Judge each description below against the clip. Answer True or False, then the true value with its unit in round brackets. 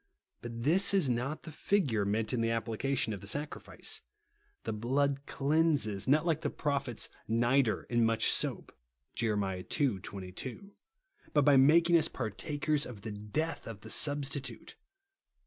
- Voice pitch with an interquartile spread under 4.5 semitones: False (4.9 semitones)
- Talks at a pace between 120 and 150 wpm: False (160 wpm)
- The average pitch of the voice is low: True (130 Hz)